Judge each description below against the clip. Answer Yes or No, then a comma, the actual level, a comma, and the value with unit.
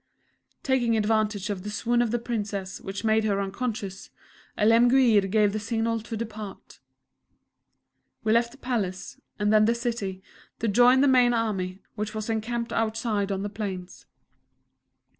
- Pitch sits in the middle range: No, high, 220 Hz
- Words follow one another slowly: No, average, 150 wpm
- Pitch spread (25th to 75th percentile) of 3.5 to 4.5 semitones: No, narrow, 2.5 semitones